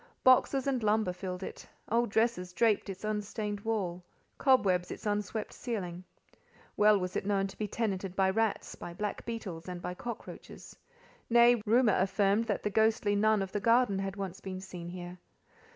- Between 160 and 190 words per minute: Yes, average, 165 wpm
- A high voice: Yes, high, 205 Hz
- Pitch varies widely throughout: No, average, 3.1 semitones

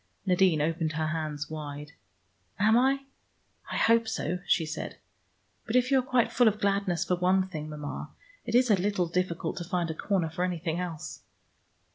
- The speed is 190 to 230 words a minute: No, average, 180 wpm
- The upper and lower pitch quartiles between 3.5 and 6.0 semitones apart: Yes, average, 4.5 semitones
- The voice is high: No, medium, 180 Hz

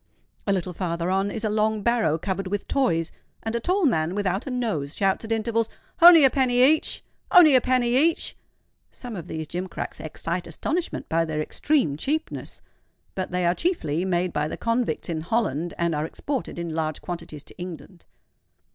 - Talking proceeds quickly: No, average, 180 wpm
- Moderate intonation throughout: No, wide, 6.5 semitones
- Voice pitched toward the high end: Yes, high, 195 Hz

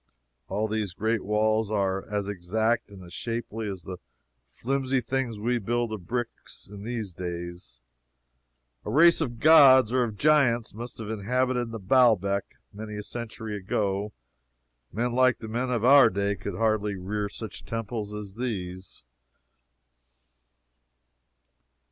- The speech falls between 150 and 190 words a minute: No, slow, 135 wpm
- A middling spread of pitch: Yes, average, 3.2 semitones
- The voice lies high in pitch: No, low, 110 Hz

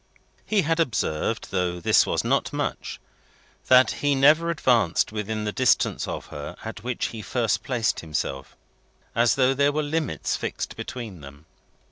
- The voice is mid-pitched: No, low, 115 Hz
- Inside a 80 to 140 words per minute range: No, average, 155 wpm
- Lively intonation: Yes, wide, 7.2 semitones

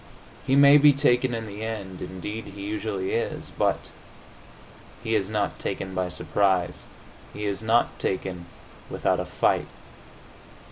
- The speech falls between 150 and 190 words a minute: No, average, 140 wpm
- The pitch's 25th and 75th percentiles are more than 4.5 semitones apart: No, average, 3.0 semitones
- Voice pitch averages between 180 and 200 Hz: No, low, 105 Hz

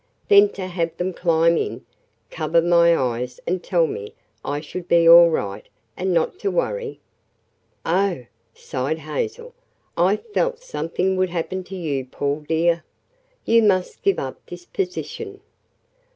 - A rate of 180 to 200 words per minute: No, average, 145 wpm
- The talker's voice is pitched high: No, medium, 175 Hz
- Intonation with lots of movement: No, average, 3.7 semitones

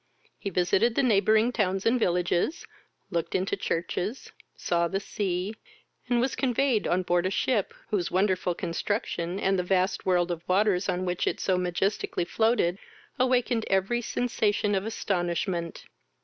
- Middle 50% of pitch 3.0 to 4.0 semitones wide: Yes, average, 3.7 semitones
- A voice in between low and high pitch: No, high, 195 Hz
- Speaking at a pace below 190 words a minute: Yes, average, 150 wpm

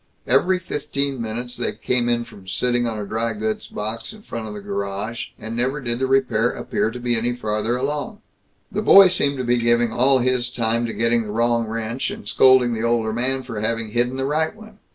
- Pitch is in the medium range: No, low, 120 Hz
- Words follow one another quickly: Yes, fast, 215 wpm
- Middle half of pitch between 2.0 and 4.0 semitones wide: Yes, average, 2.8 semitones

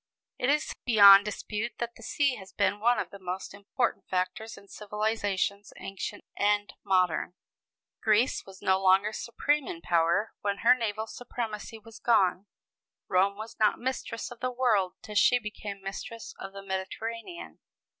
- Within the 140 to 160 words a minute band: Yes, average, 155 wpm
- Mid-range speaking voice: No, high, 210 Hz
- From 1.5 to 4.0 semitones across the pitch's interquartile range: Yes, average, 3.0 semitones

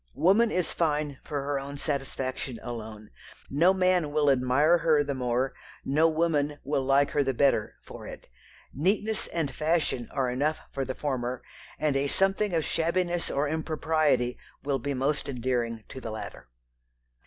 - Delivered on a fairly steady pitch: No, average, 3.6 semitones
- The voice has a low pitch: No, medium, 145 Hz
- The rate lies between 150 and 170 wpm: Yes, average, 160 wpm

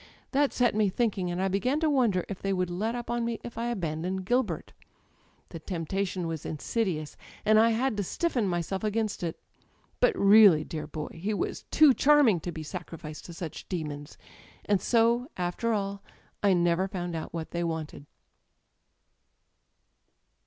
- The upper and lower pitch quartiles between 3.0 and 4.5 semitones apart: No, average, 5.2 semitones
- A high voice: Yes, high, 195 Hz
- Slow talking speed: No, average, 165 wpm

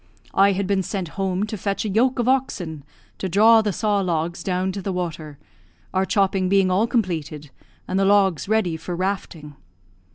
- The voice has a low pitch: No, high, 190 Hz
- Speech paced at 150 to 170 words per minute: No, average, 185 wpm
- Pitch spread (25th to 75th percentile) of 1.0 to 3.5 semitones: Yes, narrow, 2.6 semitones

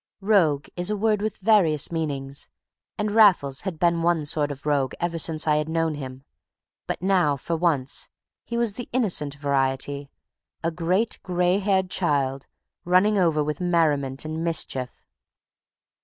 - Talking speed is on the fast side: No, average, 155 wpm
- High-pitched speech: No, medium, 165 Hz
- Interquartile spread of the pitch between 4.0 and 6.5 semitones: Yes, average, 4.4 semitones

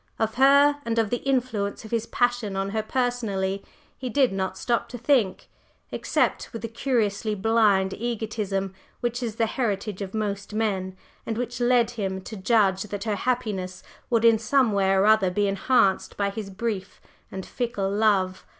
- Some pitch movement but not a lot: Yes, average, 3.3 semitones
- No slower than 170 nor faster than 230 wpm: Yes, average, 175 wpm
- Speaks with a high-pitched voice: Yes, high, 215 Hz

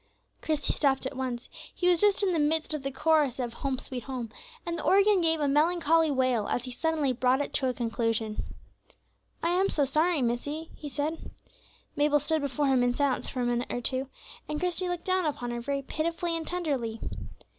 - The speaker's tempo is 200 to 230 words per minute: Yes, fast, 205 wpm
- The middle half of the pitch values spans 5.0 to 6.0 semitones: No, average, 4.2 semitones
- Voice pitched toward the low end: No, very high, 290 Hz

